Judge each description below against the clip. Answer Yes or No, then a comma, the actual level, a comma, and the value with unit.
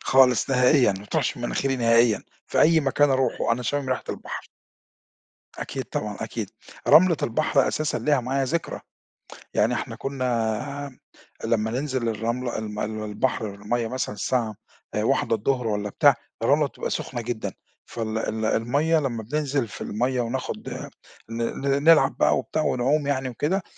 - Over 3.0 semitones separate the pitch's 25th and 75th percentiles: Yes, average, 3.5 semitones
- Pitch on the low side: Yes, low, 125 Hz